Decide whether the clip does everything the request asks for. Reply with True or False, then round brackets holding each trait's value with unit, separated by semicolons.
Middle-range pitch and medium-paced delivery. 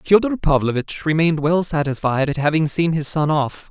True (155 Hz; 180 wpm)